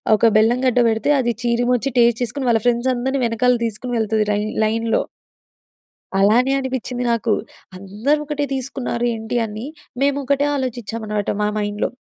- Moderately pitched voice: No, high, 235 Hz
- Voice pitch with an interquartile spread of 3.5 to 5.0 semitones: No, average, 2.9 semitones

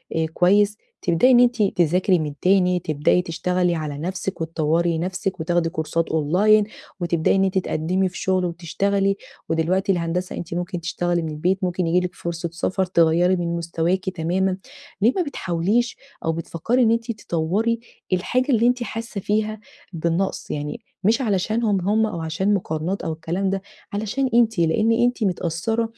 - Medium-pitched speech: Yes, medium, 180 Hz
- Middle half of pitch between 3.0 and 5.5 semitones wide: Yes, average, 3.7 semitones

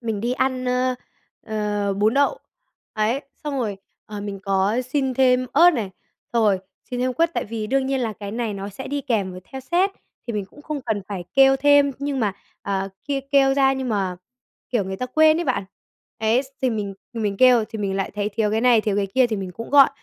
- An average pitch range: Yes, average, 4.6 semitones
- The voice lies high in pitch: Yes, high, 235 Hz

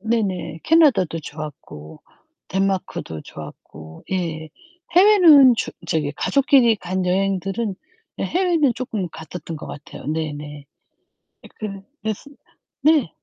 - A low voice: No, high, 190 Hz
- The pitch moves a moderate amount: No, wide, 8.1 semitones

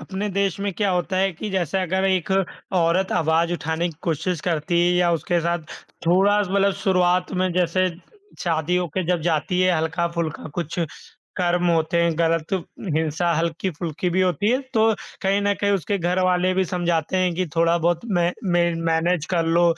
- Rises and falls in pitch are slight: Yes, narrow, 1.9 semitones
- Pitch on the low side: No, medium, 175 Hz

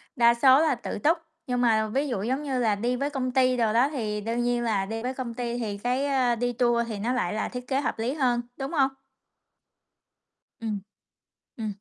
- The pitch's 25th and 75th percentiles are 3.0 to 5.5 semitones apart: No, narrow, 2.6 semitones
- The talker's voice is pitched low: No, high, 245 Hz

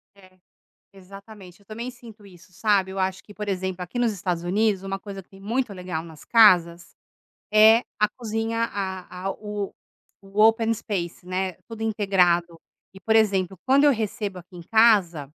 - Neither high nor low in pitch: No, high, 195 Hz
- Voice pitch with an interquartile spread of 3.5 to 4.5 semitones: No, average, 3.1 semitones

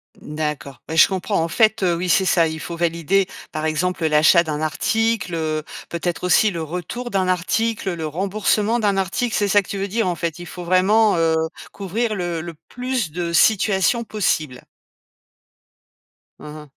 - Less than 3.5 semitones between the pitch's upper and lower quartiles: No, average, 4.2 semitones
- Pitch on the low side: No, medium, 180 Hz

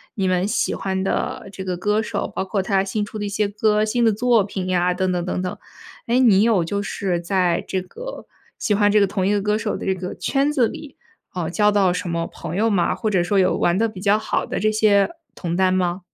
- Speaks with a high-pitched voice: Yes, high, 195 Hz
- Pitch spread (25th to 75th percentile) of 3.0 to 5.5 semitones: No, narrow, 2.5 semitones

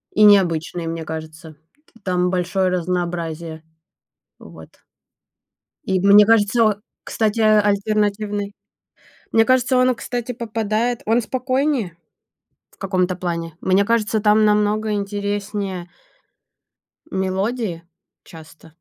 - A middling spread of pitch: Yes, average, 3.5 semitones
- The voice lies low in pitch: No, high, 200 Hz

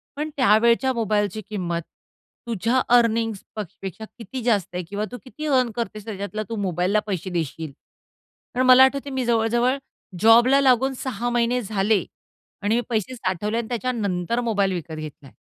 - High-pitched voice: Yes, high, 225 Hz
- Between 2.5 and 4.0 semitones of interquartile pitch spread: Yes, average, 3.7 semitones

